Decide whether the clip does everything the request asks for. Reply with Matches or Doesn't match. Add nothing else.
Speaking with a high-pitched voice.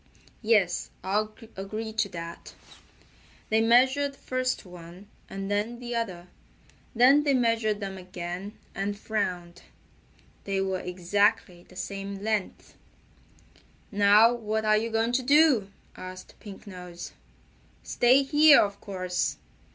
Matches